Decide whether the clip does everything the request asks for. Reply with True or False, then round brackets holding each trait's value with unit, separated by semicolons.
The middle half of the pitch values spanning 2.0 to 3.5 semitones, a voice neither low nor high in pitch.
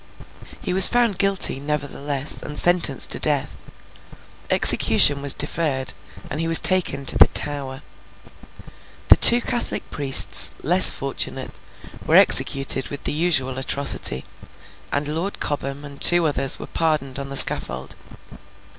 True (3.2 semitones; 145 Hz)